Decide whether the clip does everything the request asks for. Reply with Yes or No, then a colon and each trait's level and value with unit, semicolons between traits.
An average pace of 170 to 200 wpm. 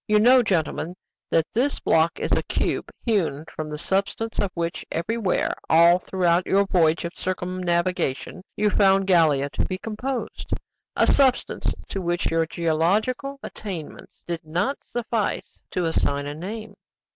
No: average, 145 wpm